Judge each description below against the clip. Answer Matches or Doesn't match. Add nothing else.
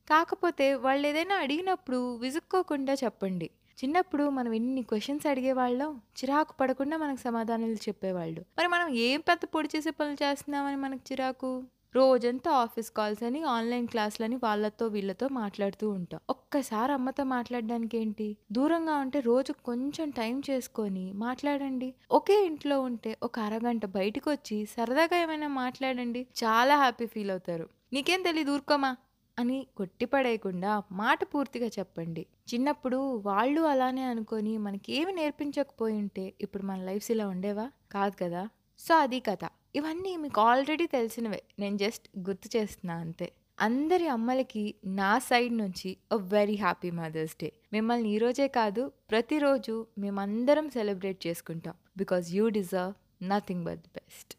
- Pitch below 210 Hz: Doesn't match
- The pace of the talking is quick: Matches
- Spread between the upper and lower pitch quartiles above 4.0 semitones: Matches